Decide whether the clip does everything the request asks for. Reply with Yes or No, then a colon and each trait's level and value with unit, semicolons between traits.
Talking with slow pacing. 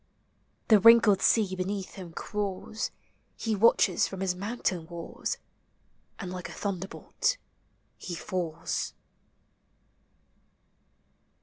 Yes: slow, 95 wpm